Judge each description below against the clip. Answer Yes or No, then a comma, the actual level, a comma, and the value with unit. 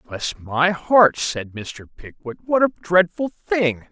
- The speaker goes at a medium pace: Yes, average, 155 wpm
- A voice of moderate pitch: Yes, medium, 165 Hz